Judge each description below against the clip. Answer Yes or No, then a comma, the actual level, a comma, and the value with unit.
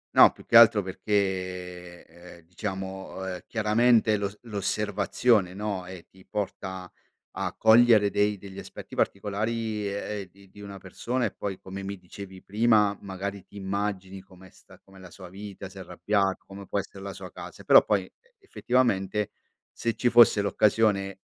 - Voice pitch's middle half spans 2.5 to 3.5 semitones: No, narrow, 1.9 semitones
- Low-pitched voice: Yes, low, 100 Hz